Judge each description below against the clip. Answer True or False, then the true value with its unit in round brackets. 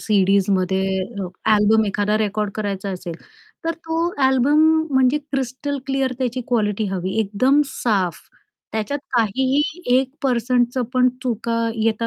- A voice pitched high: True (230 Hz)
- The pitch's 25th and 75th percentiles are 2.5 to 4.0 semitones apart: False (4.5 semitones)